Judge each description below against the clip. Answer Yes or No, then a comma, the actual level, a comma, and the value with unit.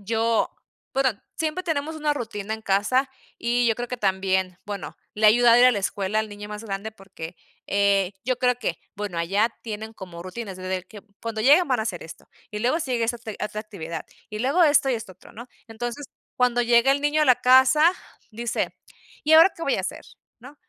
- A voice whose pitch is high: Yes, high, 225 Hz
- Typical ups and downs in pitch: Yes, average, 4.1 semitones